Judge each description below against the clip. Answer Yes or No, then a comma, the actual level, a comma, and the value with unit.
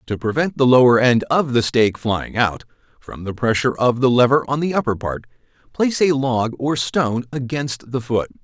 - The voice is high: No, low, 125 Hz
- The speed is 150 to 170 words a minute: No, average, 200 wpm